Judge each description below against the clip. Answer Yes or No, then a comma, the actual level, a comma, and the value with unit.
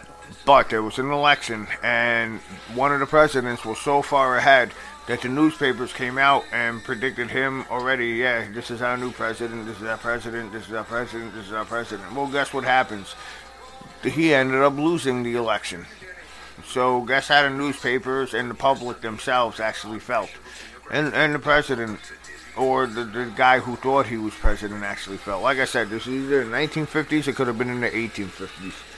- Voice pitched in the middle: No, low, 125 Hz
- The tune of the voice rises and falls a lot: No, average, 3.2 semitones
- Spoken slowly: No, average, 190 wpm